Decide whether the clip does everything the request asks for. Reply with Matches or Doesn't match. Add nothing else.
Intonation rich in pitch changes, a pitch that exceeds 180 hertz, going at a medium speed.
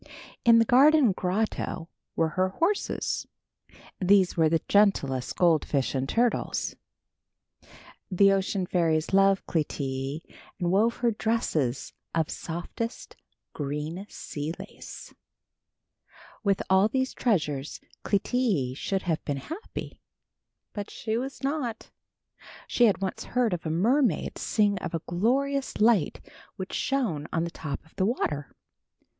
Doesn't match